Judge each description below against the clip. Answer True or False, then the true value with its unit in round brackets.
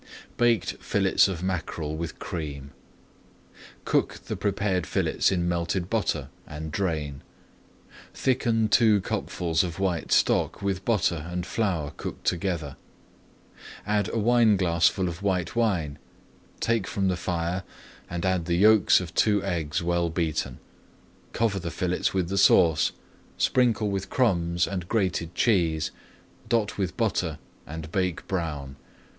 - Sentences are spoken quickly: False (135 wpm)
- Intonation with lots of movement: False (3.2 semitones)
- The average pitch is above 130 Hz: False (90 Hz)